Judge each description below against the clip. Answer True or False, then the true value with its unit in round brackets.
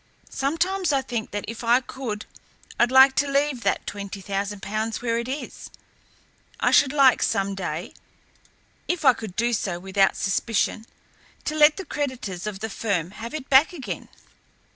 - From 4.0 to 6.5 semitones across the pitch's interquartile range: True (5.5 semitones)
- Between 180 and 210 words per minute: False (165 wpm)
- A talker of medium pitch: False (235 Hz)